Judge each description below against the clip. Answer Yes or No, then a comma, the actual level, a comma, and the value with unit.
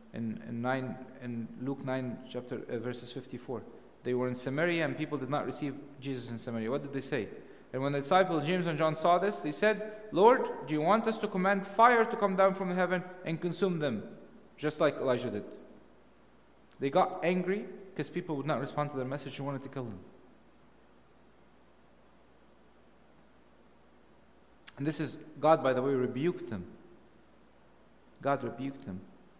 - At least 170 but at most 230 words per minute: Yes, average, 175 wpm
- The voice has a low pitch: No, medium, 145 Hz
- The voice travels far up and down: Yes, wide, 5.8 semitones